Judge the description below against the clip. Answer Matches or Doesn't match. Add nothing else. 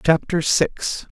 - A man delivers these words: Matches